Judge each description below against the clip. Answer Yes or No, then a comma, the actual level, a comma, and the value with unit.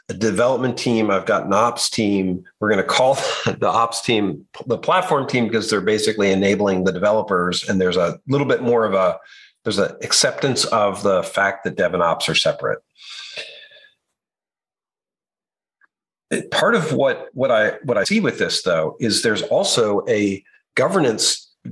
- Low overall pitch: Yes, low, 110 Hz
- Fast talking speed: No, average, 165 wpm